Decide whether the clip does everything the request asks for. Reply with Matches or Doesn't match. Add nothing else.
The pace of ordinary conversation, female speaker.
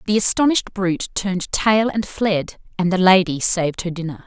Matches